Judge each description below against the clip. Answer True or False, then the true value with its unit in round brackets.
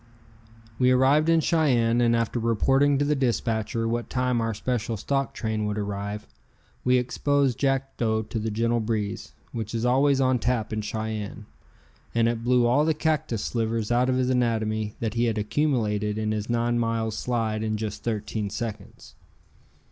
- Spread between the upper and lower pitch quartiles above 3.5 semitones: False (2.7 semitones)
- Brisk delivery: False (170 wpm)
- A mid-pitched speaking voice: False (115 Hz)